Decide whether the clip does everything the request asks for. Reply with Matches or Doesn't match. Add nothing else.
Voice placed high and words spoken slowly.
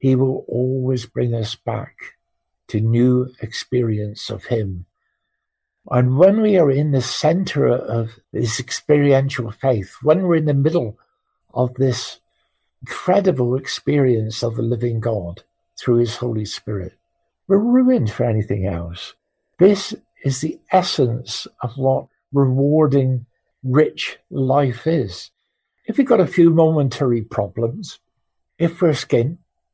Doesn't match